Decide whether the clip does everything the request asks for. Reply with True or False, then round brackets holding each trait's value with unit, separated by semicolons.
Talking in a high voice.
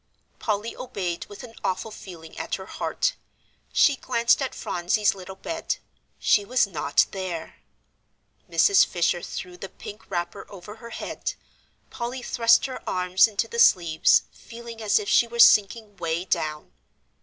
True (205 Hz)